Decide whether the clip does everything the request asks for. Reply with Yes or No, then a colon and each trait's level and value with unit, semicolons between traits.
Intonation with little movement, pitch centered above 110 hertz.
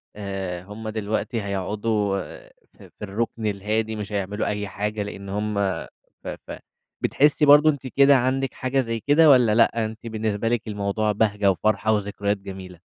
No: narrow, 2.2 semitones; low, 105 Hz